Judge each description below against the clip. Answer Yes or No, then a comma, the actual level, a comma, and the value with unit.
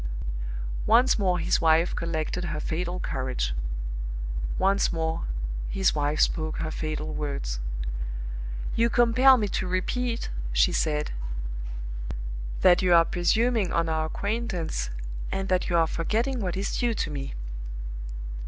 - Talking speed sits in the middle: No, slow, 130 wpm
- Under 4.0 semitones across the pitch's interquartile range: No, average, 4.7 semitones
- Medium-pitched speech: Yes, medium, 175 Hz